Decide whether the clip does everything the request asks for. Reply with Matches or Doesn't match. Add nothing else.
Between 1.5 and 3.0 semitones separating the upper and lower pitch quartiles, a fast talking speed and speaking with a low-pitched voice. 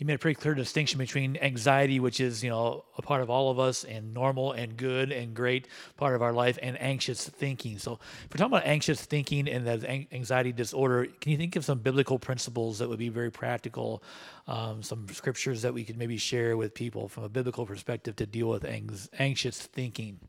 Matches